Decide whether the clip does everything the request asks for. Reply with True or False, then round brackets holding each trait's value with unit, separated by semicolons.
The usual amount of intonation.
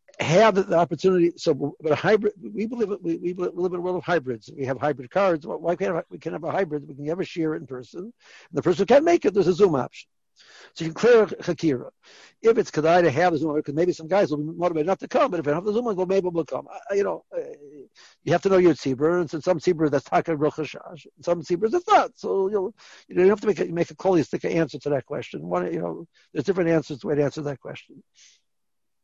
True (4.3 semitones)